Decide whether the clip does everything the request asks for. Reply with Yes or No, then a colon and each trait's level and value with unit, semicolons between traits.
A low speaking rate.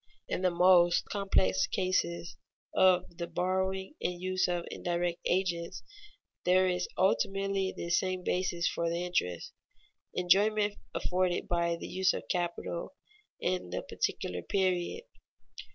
Yes: slow, 125 wpm